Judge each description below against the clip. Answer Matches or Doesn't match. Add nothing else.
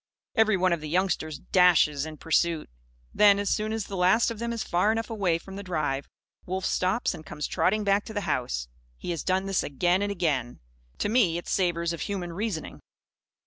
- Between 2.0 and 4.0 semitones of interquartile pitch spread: Matches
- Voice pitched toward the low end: Doesn't match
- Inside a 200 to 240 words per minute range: Matches